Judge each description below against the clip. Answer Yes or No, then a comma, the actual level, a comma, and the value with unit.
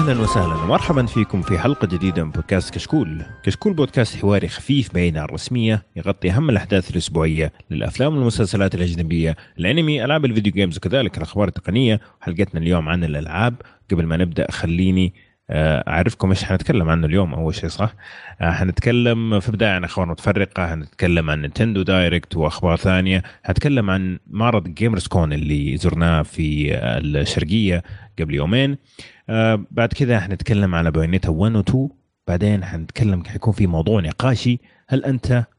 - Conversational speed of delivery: No, fast, 140 wpm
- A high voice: No, very low, 95 Hz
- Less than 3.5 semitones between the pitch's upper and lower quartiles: No, average, 4.8 semitones